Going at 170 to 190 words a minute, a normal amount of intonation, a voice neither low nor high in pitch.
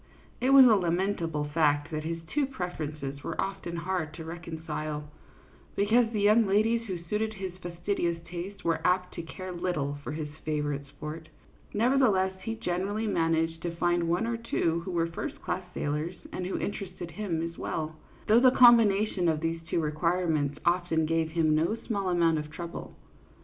Yes: average, 175 wpm; average, 3.6 semitones; medium, 170 Hz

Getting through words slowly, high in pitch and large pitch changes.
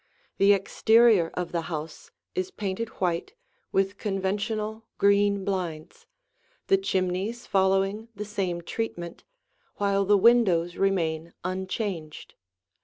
No: slow, 110 wpm; high, 195 Hz; average, 2.9 semitones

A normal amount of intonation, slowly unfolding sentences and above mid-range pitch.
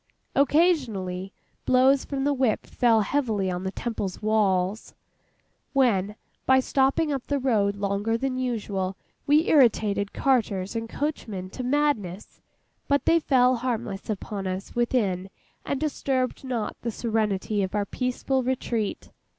Yes: average, 4.9 semitones; slow, 130 wpm; high, 230 Hz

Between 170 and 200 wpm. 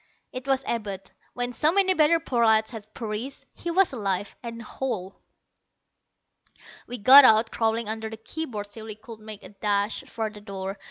Yes: average, 175 wpm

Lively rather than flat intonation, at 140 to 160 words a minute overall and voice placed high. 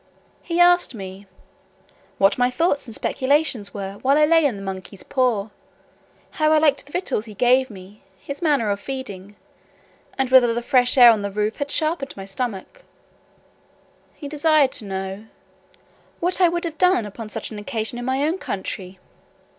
No: wide, 6.4 semitones; average, 175 wpm; very high, 250 Hz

